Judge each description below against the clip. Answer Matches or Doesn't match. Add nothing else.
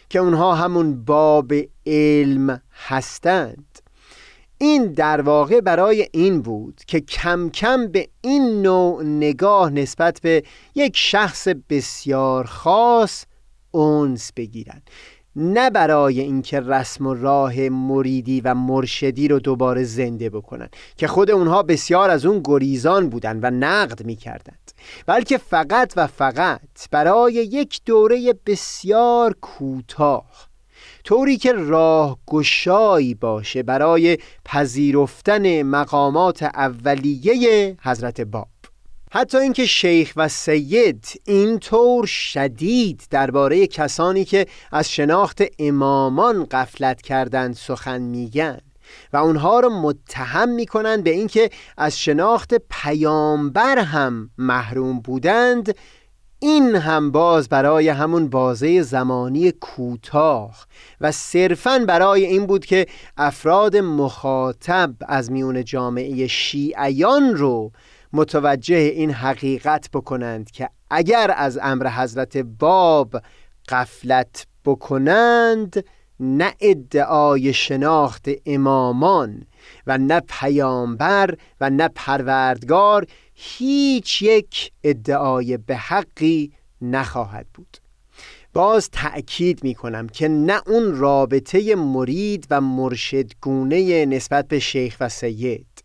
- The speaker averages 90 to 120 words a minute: Matches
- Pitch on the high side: Doesn't match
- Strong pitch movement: Matches